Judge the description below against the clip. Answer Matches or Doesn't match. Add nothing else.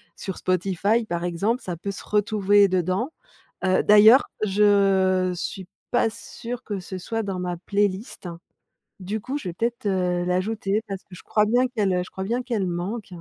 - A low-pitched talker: Doesn't match